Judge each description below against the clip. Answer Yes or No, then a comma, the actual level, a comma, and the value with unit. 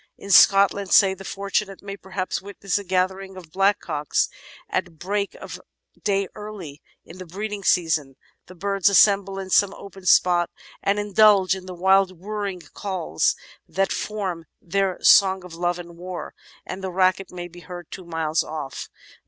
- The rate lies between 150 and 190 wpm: Yes, average, 165 wpm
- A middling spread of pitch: No, narrow, 2.1 semitones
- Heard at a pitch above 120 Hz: Yes, high, 190 Hz